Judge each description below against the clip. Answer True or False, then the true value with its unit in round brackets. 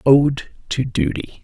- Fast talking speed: False (125 wpm)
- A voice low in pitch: True (120 Hz)